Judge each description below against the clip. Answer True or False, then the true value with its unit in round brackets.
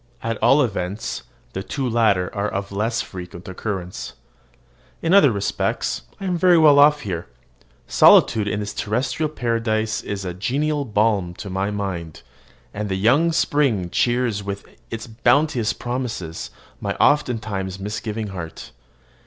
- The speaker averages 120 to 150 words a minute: True (140 wpm)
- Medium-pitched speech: False (110 Hz)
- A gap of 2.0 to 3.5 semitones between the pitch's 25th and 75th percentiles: False (4.5 semitones)